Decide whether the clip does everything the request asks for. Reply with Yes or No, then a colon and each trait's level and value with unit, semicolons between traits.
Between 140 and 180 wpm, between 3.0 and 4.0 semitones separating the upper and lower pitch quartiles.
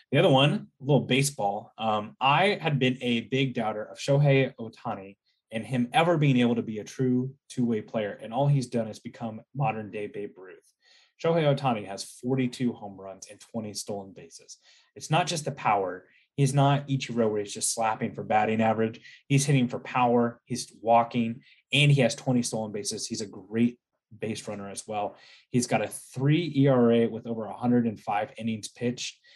No: average, 190 wpm; average, 3.4 semitones